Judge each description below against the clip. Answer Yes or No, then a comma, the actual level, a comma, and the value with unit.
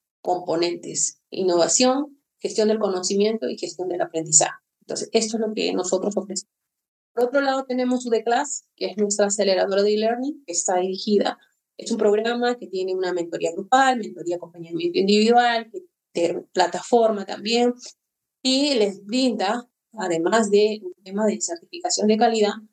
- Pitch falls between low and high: No, high, 210 Hz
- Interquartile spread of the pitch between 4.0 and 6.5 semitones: Yes, average, 4.6 semitones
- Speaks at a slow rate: No, average, 145 wpm